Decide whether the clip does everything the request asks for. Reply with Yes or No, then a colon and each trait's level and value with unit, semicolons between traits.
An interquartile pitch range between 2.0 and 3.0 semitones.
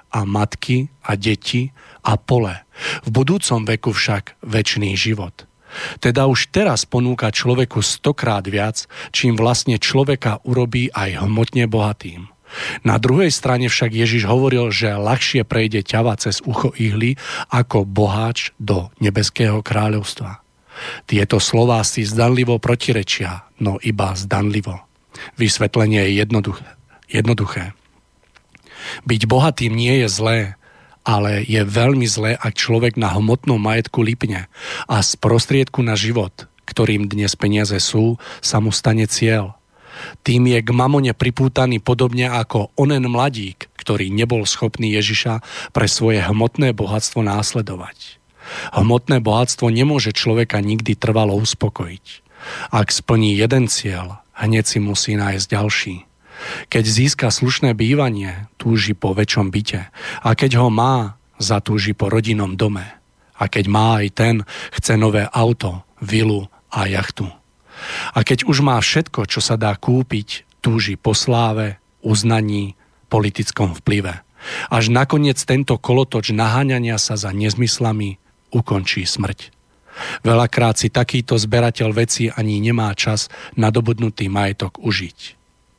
Yes: average, 2.7 semitones